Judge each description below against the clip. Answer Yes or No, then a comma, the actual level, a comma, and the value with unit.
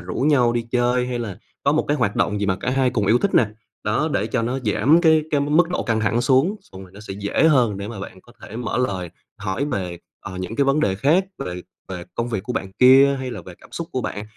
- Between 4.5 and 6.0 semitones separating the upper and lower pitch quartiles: Yes, average, 5.3 semitones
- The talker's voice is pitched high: No, low, 120 Hz